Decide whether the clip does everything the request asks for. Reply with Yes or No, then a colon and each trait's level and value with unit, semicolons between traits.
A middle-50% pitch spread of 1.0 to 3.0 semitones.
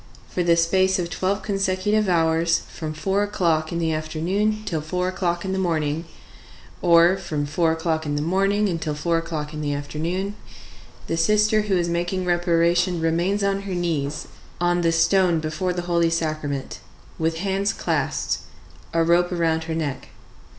Yes: narrow, 2.6 semitones